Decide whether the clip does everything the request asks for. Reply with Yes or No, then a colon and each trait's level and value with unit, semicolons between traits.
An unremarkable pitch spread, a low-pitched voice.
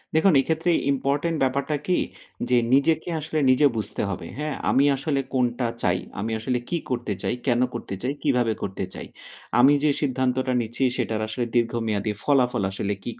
Yes: average, 3.6 semitones; low, 130 Hz